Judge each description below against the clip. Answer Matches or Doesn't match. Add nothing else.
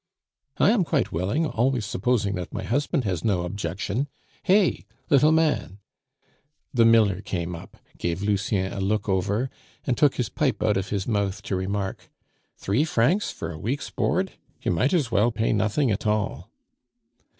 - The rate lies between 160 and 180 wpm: Matches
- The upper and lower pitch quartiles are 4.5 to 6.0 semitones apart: Matches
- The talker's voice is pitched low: Matches